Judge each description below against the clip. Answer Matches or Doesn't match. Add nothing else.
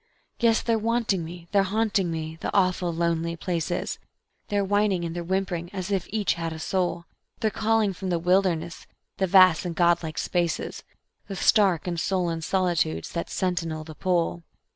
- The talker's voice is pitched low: Doesn't match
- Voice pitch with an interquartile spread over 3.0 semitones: Doesn't match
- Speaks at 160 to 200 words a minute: Matches